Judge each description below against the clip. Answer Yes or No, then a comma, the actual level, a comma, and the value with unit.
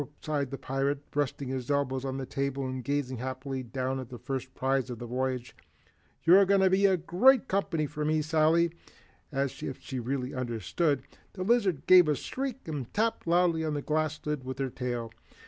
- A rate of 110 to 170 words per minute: No, average, 190 wpm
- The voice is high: No, medium, 140 Hz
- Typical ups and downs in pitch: Yes, average, 3.7 semitones